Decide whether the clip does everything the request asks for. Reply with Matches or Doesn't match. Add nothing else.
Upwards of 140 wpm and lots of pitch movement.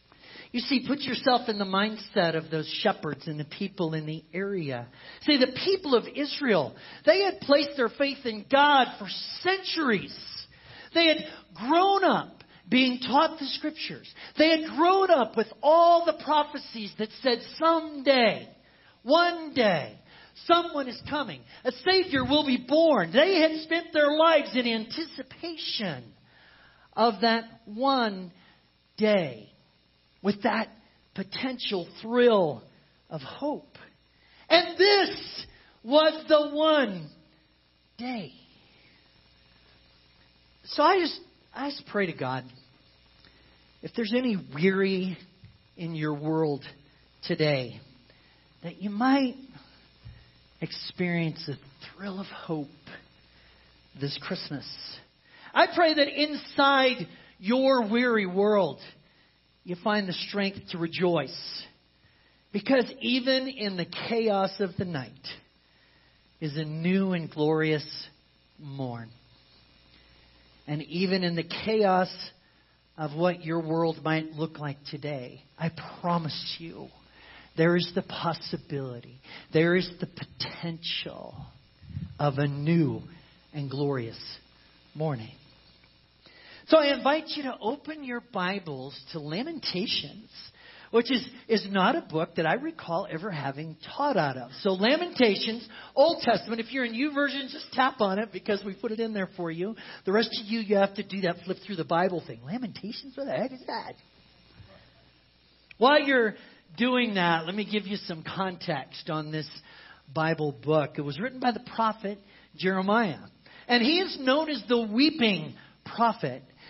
Doesn't match